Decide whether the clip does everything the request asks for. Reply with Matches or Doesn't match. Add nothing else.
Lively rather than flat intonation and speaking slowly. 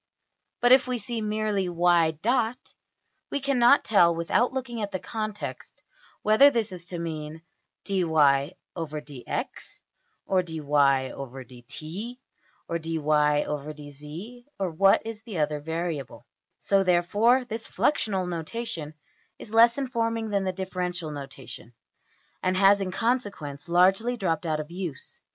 Matches